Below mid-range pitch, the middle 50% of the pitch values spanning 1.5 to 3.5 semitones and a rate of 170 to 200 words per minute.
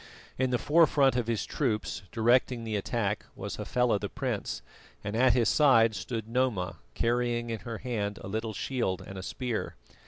Yes: low, 115 Hz; average, 2.9 semitones; average, 175 wpm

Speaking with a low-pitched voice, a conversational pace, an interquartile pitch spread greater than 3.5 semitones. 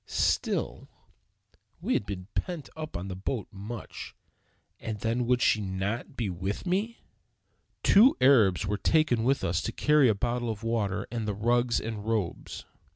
Yes: low, 115 Hz; average, 160 wpm; average, 3.9 semitones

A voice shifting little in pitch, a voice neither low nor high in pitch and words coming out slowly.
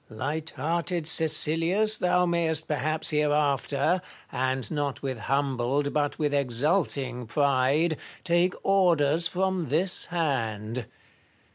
No: average, 3.9 semitones; medium, 150 Hz; slow, 105 wpm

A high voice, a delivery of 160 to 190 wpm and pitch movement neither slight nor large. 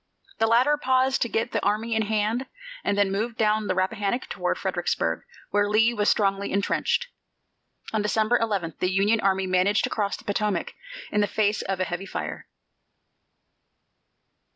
No: high, 210 Hz; average, 165 wpm; narrow, 2.2 semitones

